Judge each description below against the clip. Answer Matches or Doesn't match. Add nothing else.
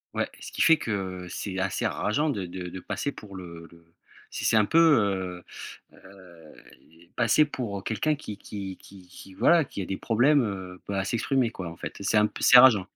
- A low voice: Matches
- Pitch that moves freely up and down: Doesn't match